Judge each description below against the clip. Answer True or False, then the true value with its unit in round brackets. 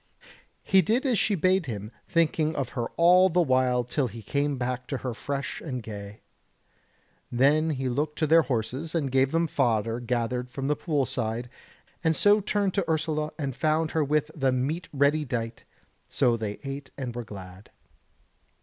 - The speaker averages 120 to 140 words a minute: False (175 wpm)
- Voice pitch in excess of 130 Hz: True (140 Hz)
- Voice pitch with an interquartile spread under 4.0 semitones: False (4.4 semitones)